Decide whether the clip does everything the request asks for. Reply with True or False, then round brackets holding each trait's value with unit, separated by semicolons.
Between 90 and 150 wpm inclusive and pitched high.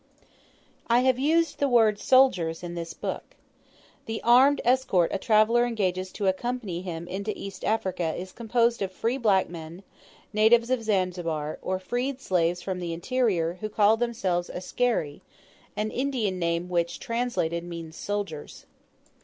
True (145 wpm; 200 Hz)